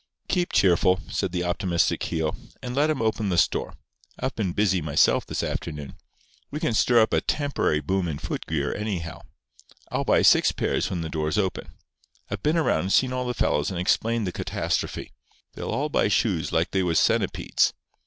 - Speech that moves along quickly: No, average, 190 wpm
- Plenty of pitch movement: Yes, wide, 5.9 semitones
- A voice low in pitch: Yes, very low, 95 Hz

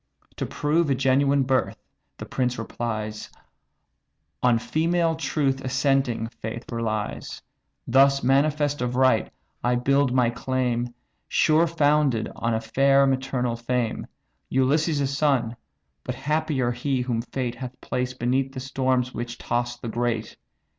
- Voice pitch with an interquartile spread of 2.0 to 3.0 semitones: Yes, narrow, 2.4 semitones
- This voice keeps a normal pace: No, slow, 130 wpm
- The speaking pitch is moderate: No, low, 130 Hz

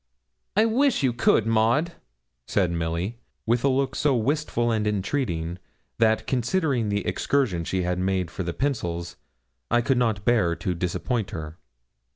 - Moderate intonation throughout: No, wide, 6.5 semitones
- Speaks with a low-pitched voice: Yes, low, 110 Hz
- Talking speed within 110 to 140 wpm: No, average, 155 wpm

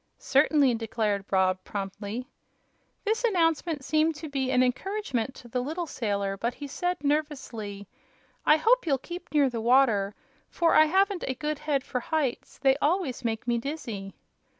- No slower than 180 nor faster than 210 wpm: No, average, 160 wpm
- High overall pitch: Yes, very high, 270 Hz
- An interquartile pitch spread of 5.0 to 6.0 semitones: Yes, wide, 5.4 semitones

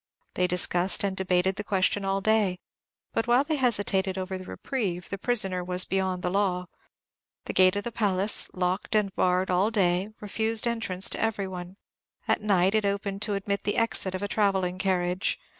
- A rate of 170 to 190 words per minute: Yes, average, 185 wpm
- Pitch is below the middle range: No, high, 195 Hz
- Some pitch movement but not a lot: No, narrow, 2.3 semitones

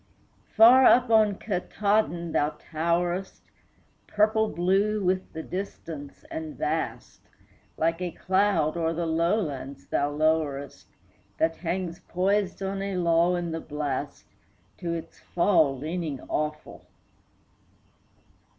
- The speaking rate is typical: No, slow, 115 wpm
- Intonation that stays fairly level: No, average, 3.5 semitones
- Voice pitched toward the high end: No, medium, 170 Hz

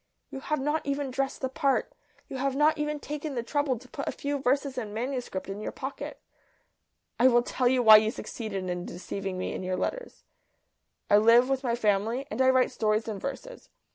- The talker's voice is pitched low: No, very high, 255 Hz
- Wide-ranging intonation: No, average, 4.3 semitones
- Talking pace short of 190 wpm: No, fast, 205 wpm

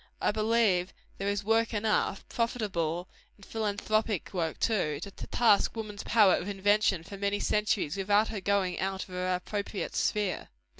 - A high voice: Yes, high, 200 Hz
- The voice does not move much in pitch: Yes, narrow, 2.3 semitones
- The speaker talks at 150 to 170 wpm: Yes, average, 155 wpm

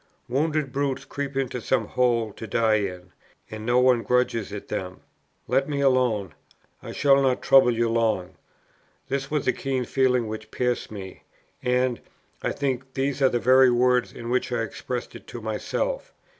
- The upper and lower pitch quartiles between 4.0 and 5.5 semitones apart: No, average, 2.9 semitones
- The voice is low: Yes, low, 125 Hz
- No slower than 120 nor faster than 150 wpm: No, average, 170 wpm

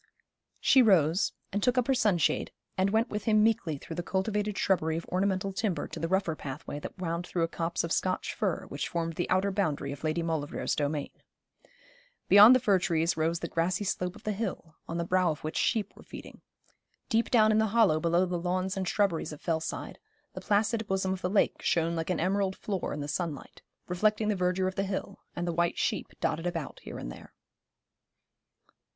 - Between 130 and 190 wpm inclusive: No, fast, 205 wpm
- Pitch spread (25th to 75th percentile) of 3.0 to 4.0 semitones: Yes, average, 3.6 semitones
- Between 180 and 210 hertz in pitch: Yes, medium, 185 Hz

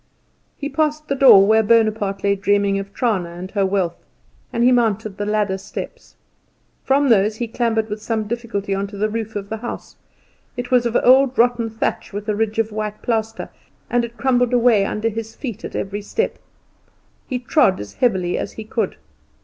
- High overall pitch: Yes, high, 220 Hz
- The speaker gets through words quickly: No, average, 190 wpm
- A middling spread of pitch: Yes, average, 3.0 semitones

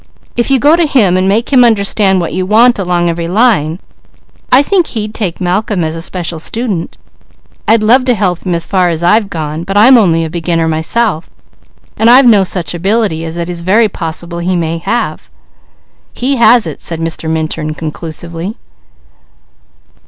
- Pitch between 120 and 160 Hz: No, medium, 185 Hz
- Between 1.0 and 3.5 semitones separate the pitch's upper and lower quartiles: No, average, 5.3 semitones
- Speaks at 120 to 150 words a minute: No, average, 180 wpm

